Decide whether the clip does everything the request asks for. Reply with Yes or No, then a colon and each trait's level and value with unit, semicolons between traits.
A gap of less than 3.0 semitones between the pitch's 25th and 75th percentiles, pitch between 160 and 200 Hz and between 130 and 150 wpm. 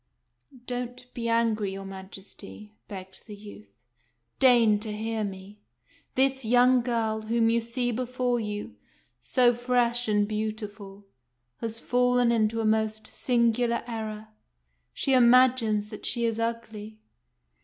No: narrow, 2.5 semitones; high, 225 Hz; slow, 135 wpm